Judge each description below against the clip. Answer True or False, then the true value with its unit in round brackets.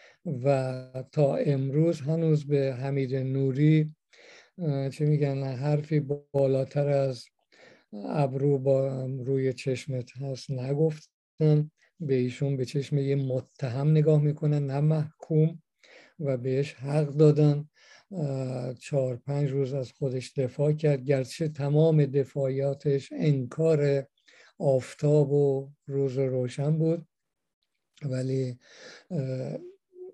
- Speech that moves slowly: True (100 wpm)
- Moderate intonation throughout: False (2.1 semitones)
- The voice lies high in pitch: False (140 Hz)